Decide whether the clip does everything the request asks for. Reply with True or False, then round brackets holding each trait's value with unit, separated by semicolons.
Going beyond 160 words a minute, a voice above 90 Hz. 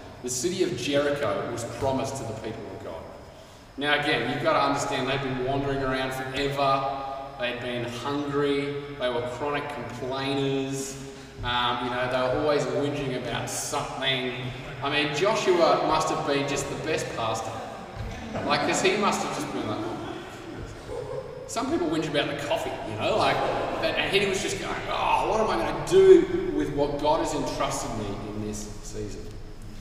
True (175 wpm; 135 Hz)